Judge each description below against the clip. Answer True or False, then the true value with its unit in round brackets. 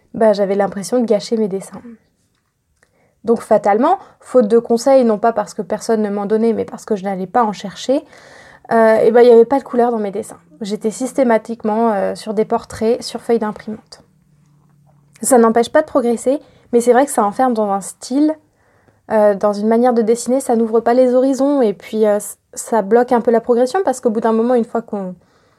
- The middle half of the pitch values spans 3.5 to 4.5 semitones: False (2.4 semitones)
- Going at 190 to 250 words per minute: True (215 wpm)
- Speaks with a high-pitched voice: True (230 Hz)